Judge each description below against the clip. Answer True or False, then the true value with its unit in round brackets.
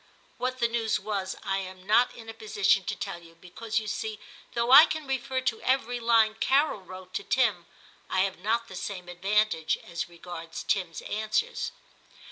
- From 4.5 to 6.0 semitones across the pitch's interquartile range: False (4.1 semitones)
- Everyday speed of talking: True (180 wpm)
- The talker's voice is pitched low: False (215 Hz)